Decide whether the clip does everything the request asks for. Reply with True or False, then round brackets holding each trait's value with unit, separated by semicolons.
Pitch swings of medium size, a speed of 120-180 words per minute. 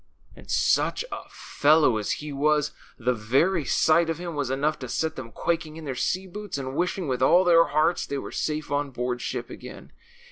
False (4.0 semitones; 205 wpm)